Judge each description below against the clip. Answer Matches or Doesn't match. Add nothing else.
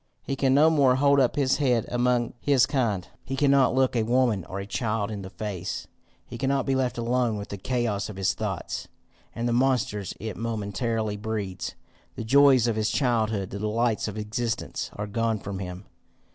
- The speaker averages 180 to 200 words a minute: Matches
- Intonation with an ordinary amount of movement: Matches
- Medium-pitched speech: Doesn't match